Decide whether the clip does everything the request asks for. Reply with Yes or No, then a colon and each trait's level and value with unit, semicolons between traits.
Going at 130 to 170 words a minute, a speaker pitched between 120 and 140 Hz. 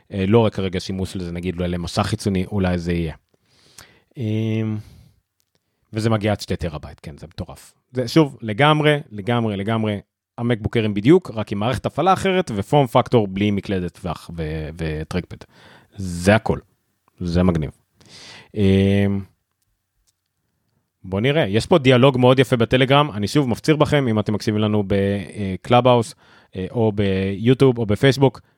No: average, 135 wpm; low, 105 Hz